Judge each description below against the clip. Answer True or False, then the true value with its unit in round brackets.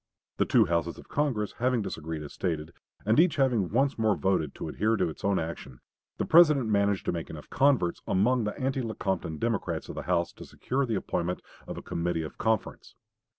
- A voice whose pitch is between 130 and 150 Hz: False (100 Hz)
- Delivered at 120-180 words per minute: False (200 wpm)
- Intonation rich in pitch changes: True (6.6 semitones)